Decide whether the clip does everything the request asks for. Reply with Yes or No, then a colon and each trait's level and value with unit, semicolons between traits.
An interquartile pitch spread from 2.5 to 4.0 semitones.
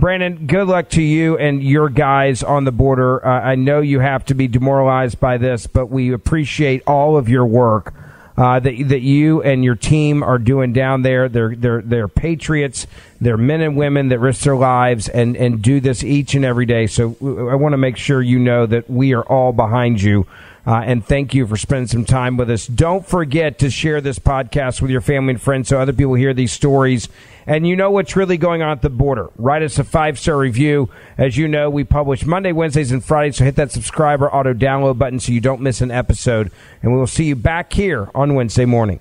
Yes: average, 2.8 semitones